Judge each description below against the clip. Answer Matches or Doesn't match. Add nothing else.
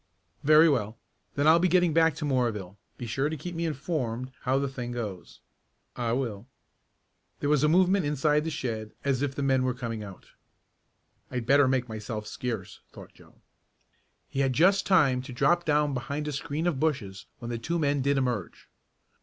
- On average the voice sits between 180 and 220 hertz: Doesn't match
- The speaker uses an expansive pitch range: Doesn't match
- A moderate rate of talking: Matches